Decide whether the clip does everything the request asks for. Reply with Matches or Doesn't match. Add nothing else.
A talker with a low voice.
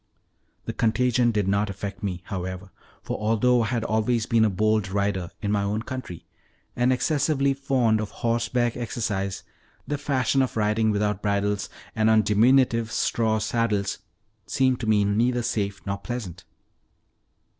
Matches